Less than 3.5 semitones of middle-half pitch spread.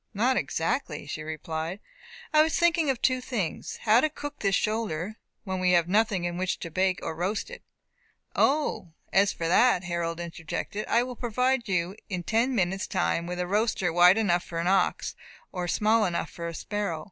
No: average, 4.9 semitones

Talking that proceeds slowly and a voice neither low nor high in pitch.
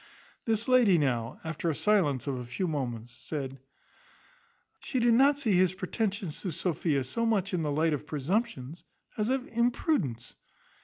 No: average, 155 wpm; medium, 175 Hz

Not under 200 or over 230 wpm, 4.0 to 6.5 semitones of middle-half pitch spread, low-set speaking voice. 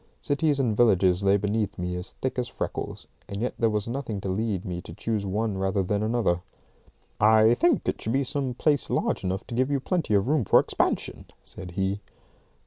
Yes: fast, 205 wpm; average, 4.5 semitones; low, 110 Hz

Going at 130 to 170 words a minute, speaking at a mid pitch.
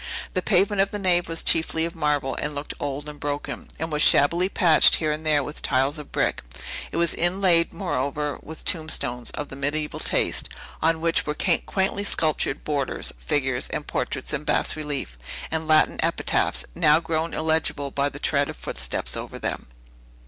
No: average, 180 wpm; medium, 155 Hz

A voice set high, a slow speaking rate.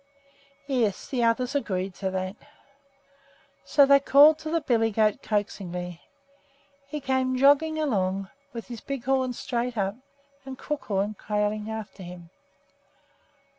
Yes: high, 230 Hz; slow, 130 wpm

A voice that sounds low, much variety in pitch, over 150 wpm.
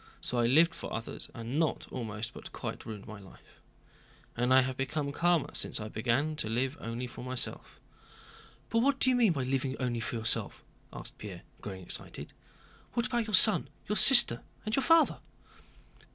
Yes: low, 130 Hz; wide, 7.0 semitones; average, 180 wpm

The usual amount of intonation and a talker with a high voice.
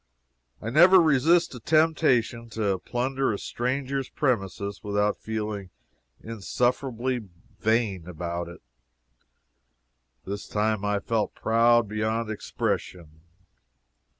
No: average, 3.9 semitones; low, 110 Hz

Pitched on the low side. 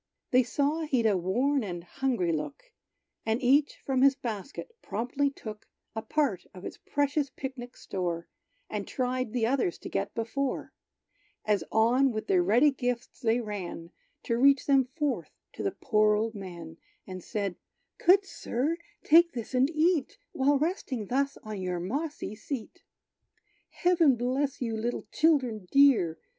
No: high, 245 Hz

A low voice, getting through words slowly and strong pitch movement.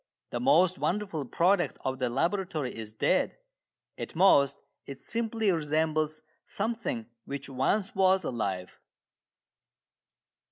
No: medium, 160 Hz; slow, 110 wpm; wide, 6.3 semitones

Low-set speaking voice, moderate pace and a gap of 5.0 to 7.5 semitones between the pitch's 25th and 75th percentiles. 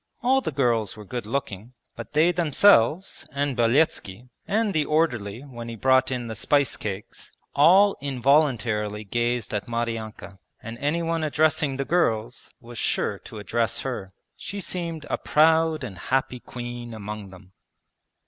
Yes: low, 125 Hz; average, 150 wpm; wide, 5.4 semitones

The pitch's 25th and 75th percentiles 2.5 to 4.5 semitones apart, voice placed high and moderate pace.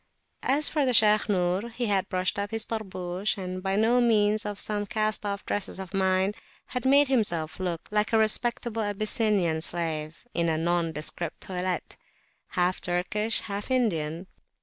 Yes: average, 3.6 semitones; high, 200 Hz; average, 150 wpm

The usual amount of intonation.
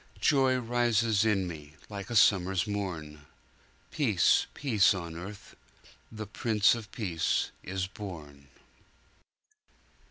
Yes: average, 4.4 semitones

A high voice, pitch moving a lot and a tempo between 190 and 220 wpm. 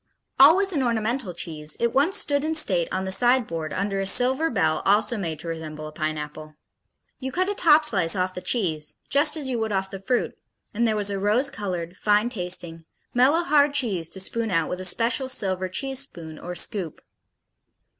Yes: high, 205 Hz; wide, 7.1 semitones; average, 200 wpm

